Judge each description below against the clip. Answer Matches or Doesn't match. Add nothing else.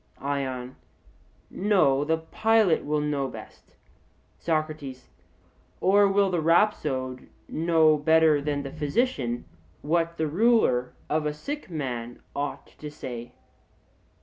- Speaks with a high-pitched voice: Doesn't match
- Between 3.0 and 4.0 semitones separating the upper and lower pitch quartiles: Matches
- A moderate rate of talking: Doesn't match